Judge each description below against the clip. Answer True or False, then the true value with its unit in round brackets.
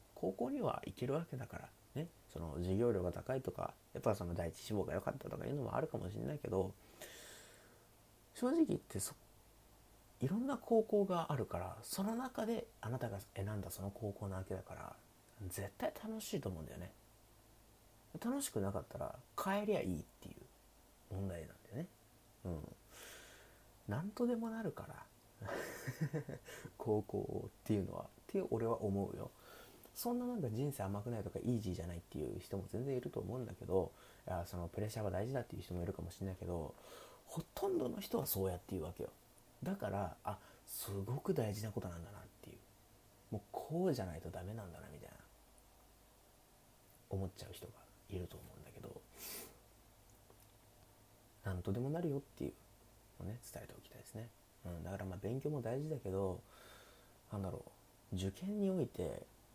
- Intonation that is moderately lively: True (4.9 semitones)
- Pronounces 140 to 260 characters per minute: False (345 characters per minute)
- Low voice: True (110 Hz)